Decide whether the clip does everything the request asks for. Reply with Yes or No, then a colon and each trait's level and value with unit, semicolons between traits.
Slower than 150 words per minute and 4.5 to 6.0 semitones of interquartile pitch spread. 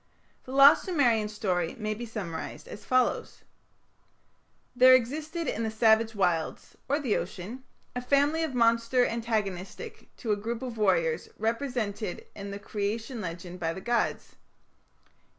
No: average, 140 wpm; average, 4.1 semitones